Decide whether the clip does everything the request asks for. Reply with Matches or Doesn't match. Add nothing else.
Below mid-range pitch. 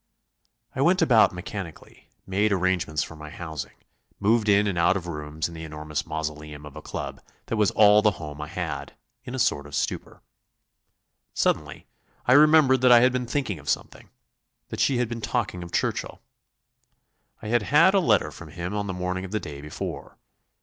Matches